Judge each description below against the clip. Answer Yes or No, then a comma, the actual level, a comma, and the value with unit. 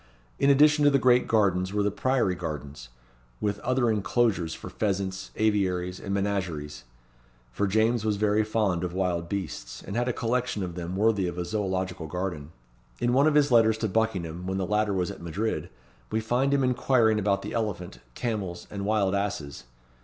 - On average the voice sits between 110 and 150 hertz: No, low, 100 Hz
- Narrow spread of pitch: No, average, 3.6 semitones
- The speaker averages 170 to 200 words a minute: Yes, average, 185 wpm